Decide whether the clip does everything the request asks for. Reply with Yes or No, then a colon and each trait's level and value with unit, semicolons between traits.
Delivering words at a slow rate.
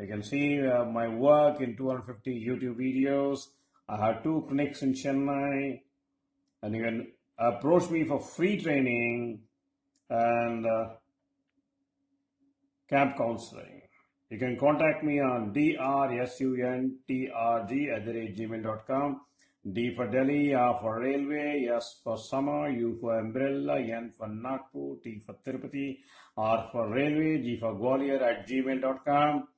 Yes: slow, 125 wpm